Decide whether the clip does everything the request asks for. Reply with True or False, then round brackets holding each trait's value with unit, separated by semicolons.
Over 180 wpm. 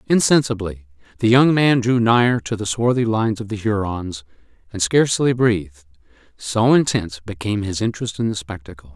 False (160 wpm)